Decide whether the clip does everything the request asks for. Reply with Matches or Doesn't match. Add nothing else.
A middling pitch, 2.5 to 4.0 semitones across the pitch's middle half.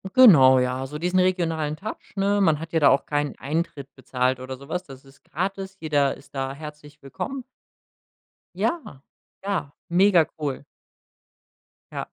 Doesn't match